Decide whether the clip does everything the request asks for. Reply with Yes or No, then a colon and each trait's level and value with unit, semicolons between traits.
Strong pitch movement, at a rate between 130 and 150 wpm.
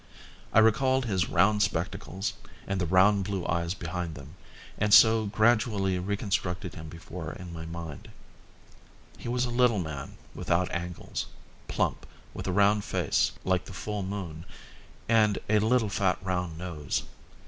No: average, 3.7 semitones; average, 145 wpm